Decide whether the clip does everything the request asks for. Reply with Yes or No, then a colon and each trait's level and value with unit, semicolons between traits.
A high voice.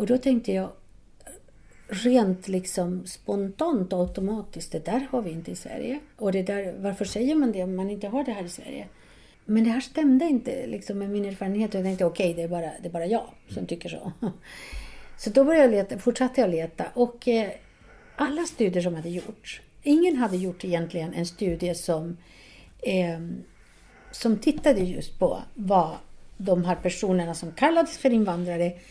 Yes: high, 200 Hz